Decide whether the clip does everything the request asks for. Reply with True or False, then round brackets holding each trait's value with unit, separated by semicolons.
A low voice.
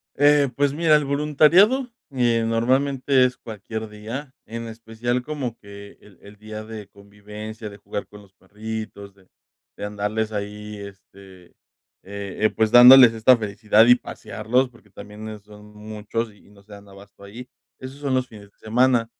True (110 Hz)